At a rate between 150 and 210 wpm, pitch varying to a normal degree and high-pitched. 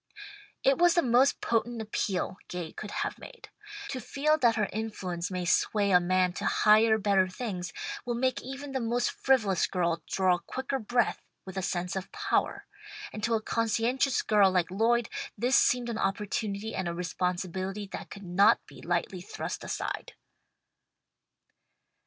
Yes: average, 160 wpm; average, 4.5 semitones; high, 210 Hz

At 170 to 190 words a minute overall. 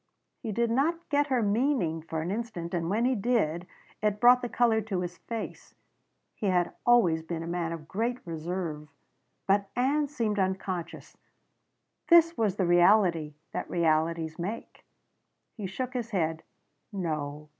No: average, 155 wpm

